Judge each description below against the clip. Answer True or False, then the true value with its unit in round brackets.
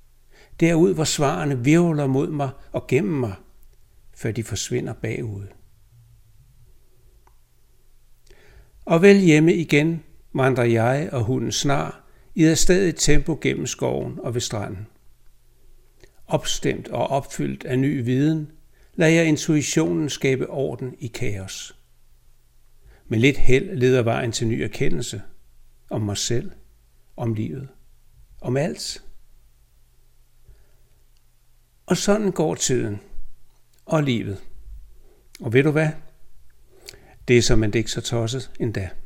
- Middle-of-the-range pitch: False (125 Hz)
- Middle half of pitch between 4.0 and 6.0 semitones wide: True (5.0 semitones)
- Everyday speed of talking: False (120 wpm)